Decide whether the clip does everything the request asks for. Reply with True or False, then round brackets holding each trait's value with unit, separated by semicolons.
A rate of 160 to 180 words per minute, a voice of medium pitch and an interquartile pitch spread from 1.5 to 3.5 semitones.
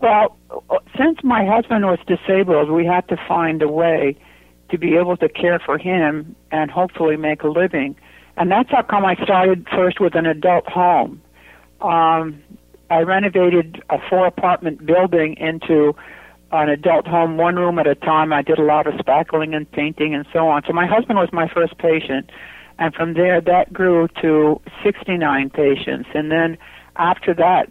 True (175 wpm; 165 Hz; 2.7 semitones)